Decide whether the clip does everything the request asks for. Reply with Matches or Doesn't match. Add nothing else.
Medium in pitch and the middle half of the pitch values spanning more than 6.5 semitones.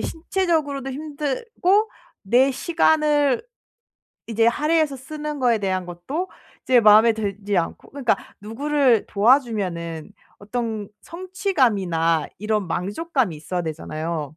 Doesn't match